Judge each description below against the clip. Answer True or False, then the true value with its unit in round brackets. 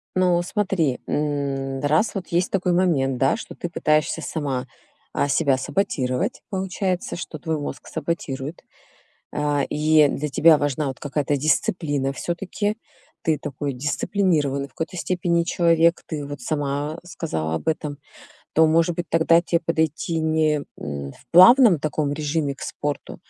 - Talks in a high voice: False (155 Hz)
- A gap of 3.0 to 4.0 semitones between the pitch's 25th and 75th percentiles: True (3.3 semitones)